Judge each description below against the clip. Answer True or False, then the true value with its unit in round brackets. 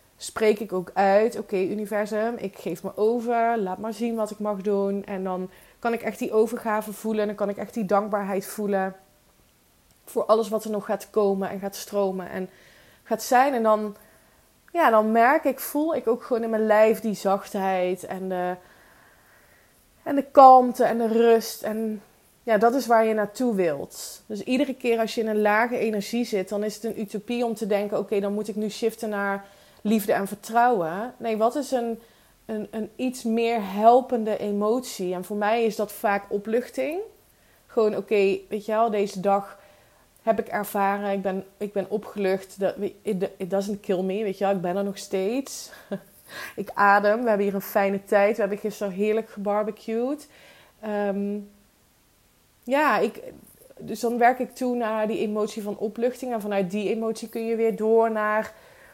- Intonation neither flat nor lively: False (2.3 semitones)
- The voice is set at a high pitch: True (215 Hz)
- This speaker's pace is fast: False (190 wpm)